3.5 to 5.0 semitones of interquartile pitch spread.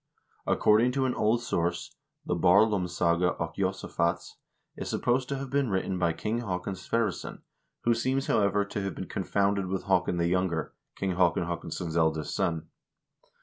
Yes: average, 4.2 semitones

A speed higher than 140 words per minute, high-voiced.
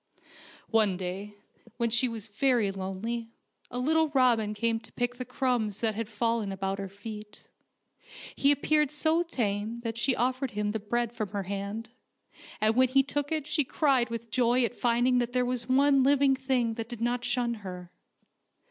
Yes: average, 180 wpm; high, 235 Hz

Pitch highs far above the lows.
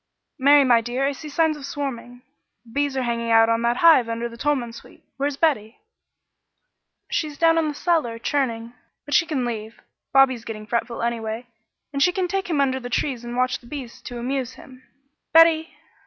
No: average, 3.7 semitones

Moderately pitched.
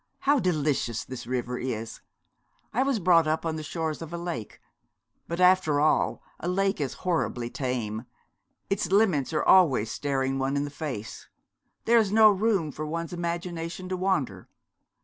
Yes: medium, 160 Hz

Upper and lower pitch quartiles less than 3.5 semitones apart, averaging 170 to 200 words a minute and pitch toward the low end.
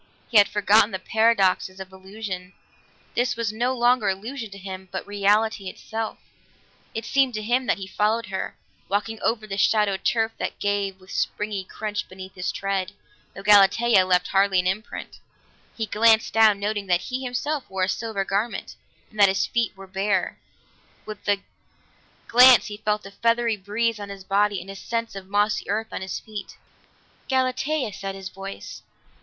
No: average, 2.7 semitones; average, 175 wpm; high, 205 Hz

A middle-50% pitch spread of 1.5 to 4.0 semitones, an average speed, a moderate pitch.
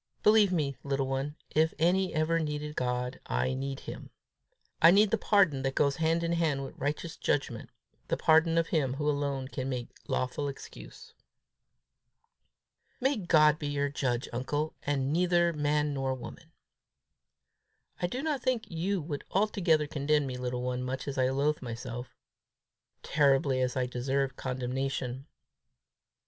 Yes: average, 3.7 semitones; average, 150 wpm; medium, 145 Hz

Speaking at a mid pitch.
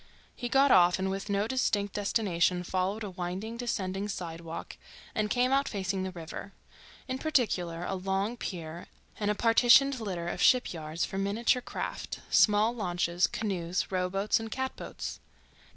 No: high, 195 Hz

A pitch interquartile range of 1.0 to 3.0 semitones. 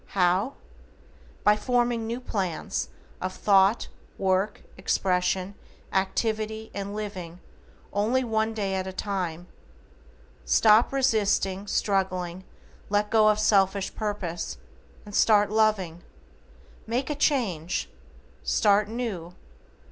Yes: average, 2.7 semitones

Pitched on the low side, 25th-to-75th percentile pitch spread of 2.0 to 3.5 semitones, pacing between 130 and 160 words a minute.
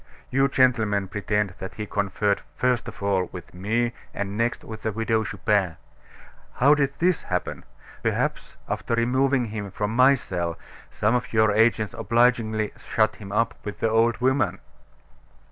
Yes: low, 110 Hz; average, 3.0 semitones; average, 155 wpm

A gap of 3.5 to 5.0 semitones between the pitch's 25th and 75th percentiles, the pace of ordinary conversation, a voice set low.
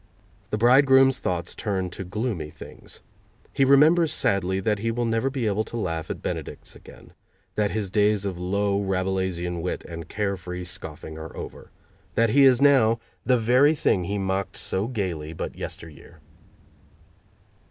Yes: average, 4.7 semitones; average, 160 wpm; low, 100 Hz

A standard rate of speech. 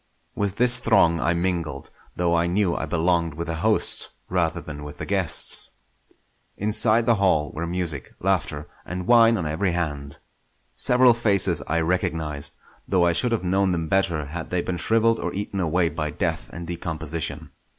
Yes: average, 170 wpm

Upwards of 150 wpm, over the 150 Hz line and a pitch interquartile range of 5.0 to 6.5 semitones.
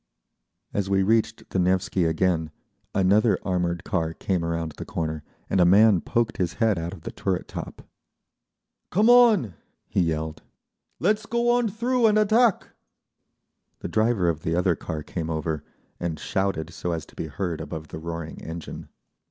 No: average, 165 wpm; very low, 90 Hz; wide, 5.5 semitones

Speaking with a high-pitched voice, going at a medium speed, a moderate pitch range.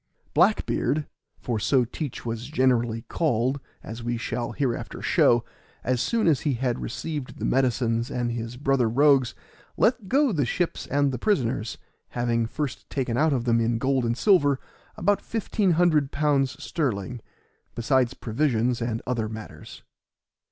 No: low, 125 Hz; average, 145 wpm; average, 3.8 semitones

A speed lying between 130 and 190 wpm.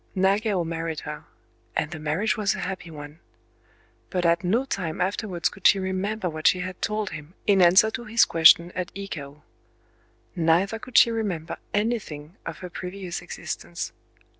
Yes: average, 165 wpm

